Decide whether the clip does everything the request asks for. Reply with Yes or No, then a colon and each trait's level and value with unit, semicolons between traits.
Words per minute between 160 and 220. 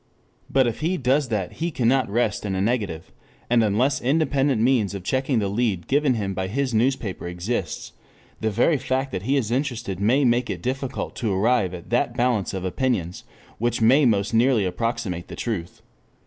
Yes: average, 185 wpm